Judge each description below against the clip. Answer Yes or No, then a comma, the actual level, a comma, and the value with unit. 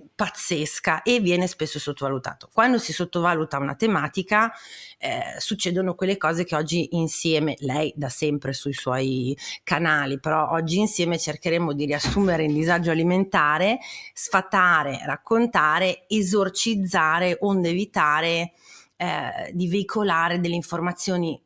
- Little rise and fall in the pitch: No, average, 4.4 semitones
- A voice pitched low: No, medium, 175 Hz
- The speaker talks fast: No, slow, 115 wpm